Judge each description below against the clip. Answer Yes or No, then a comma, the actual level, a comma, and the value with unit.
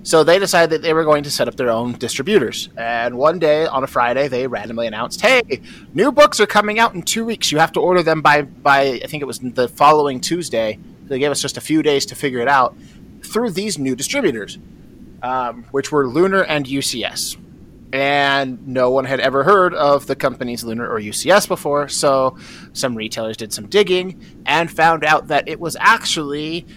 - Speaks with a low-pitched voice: No, medium, 145 Hz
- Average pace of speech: No, fast, 210 wpm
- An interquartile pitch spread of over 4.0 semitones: Yes, average, 4.5 semitones